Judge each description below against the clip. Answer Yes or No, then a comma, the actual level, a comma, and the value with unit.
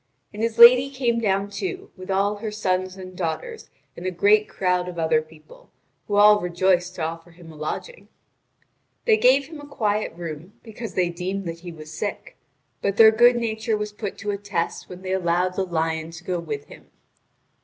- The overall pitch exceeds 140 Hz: Yes, high, 190 Hz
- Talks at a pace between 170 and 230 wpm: Yes, average, 195 wpm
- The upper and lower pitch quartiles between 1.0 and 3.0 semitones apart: No, average, 4.1 semitones